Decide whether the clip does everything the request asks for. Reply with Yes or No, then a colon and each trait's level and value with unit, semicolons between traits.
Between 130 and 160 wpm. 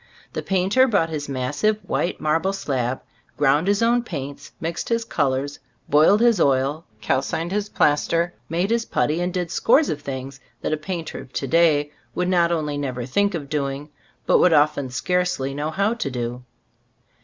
No: average, 180 wpm